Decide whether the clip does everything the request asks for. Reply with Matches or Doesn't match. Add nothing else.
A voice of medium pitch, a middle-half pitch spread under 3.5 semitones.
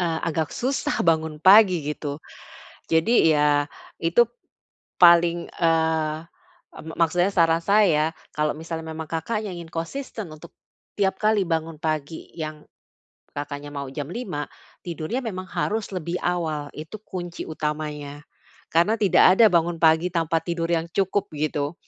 Matches